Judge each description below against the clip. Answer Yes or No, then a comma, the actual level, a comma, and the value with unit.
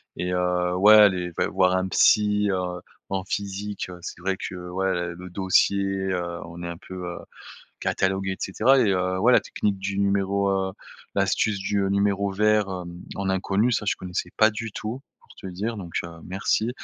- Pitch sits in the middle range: No, very low, 95 Hz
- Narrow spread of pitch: Yes, narrow, 1.9 semitones